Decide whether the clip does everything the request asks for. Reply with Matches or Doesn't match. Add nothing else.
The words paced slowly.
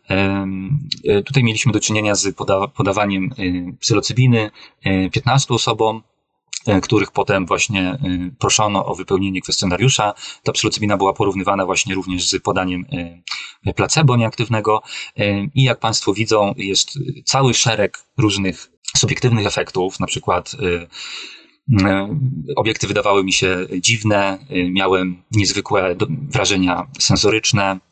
Matches